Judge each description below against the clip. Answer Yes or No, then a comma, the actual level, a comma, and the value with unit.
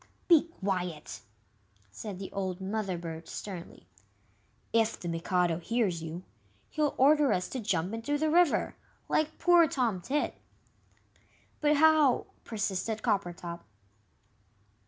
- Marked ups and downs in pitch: Yes, wide, 8.2 semitones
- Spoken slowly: Yes, slow, 120 wpm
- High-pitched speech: Yes, high, 205 Hz